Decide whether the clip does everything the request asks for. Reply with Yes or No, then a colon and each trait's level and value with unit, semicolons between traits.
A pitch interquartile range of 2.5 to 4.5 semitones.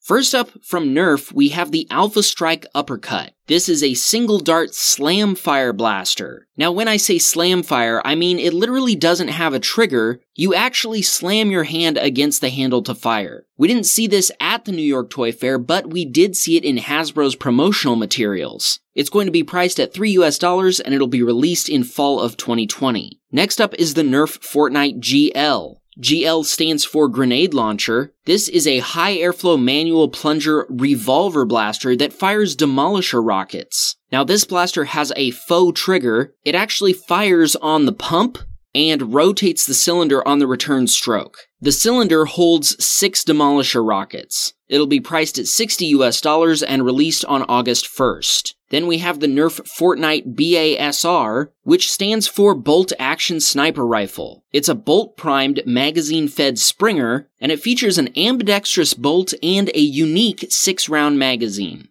No: average, 5.3 semitones